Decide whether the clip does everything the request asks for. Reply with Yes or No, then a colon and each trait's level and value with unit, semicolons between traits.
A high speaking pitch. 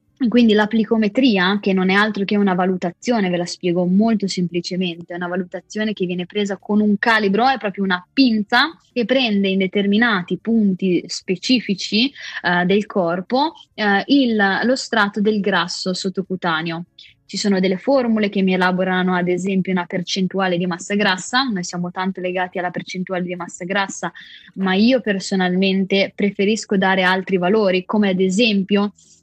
Yes: high, 195 Hz